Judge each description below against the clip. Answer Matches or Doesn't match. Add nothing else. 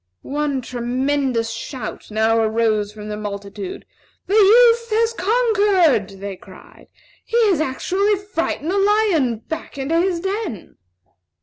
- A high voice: Matches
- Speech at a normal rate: Doesn't match